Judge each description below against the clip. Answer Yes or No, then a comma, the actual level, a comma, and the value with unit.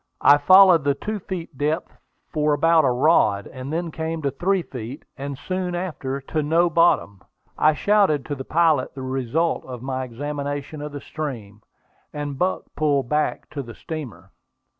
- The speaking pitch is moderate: Yes, medium, 145 Hz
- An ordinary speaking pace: Yes, average, 170 wpm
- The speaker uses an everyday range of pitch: Yes, average, 3.7 semitones